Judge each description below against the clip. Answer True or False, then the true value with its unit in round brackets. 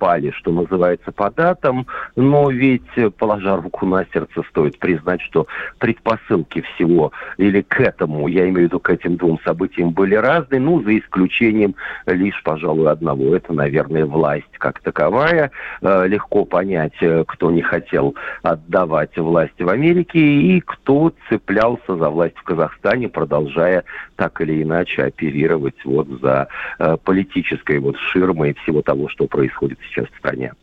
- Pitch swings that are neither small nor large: False (5.9 semitones)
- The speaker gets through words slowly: False (145 wpm)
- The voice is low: True (95 Hz)